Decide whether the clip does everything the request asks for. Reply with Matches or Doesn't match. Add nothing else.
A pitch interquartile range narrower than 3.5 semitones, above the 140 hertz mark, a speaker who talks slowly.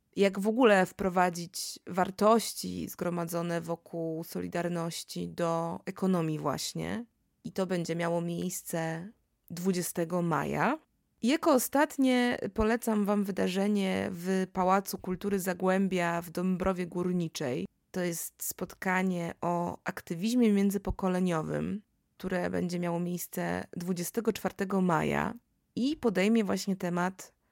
Matches